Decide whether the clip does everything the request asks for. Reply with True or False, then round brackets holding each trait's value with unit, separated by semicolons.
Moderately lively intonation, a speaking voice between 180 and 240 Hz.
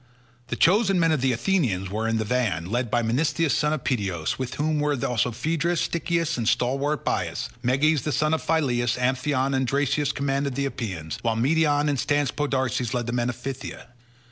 False (3.8 semitones; 135 Hz)